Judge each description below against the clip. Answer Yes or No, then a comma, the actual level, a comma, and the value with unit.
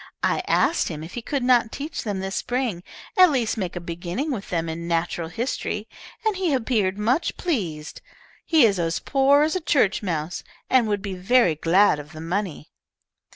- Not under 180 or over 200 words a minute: Yes, average, 190 wpm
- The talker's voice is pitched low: No, high, 205 Hz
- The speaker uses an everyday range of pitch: No, wide, 7.2 semitones